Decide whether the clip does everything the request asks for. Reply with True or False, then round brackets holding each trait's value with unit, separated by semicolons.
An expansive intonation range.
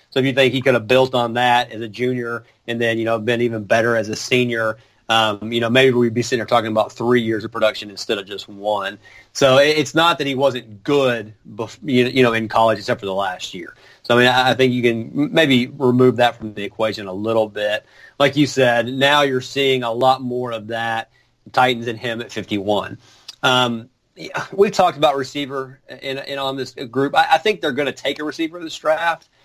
False (3.0 semitones)